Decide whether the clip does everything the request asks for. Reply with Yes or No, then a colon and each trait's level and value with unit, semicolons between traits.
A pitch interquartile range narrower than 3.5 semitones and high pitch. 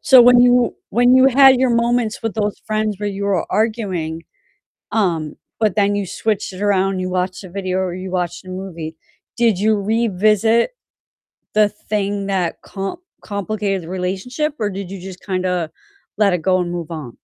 Yes: average, 2.9 semitones; high, 200 Hz